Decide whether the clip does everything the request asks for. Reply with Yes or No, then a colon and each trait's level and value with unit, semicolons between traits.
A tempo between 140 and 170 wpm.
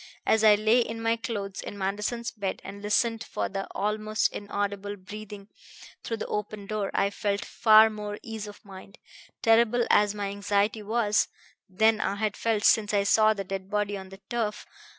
No: average, 180 wpm